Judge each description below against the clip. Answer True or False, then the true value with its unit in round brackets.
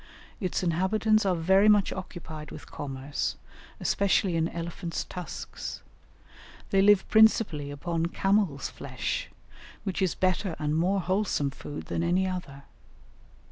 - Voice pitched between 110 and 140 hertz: False (180 Hz)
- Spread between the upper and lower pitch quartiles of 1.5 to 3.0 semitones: False (3.7 semitones)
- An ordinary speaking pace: False (125 wpm)